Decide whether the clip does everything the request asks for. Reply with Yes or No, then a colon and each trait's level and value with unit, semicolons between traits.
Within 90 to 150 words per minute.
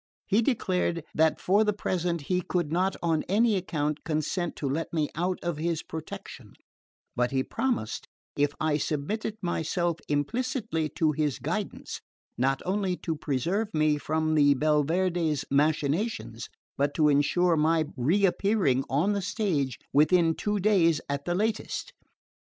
Yes: average, 145 wpm